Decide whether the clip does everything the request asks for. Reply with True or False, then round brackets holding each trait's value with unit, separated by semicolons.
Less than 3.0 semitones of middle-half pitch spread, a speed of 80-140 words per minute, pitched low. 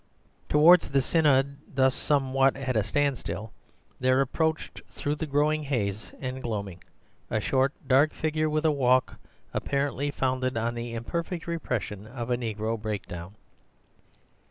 False (3.9 semitones; 135 wpm; 130 Hz)